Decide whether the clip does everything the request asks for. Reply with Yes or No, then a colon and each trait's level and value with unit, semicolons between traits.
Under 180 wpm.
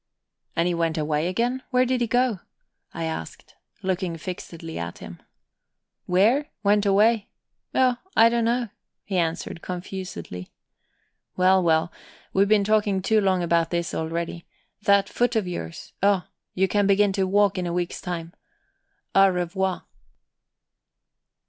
Yes: average, 140 wpm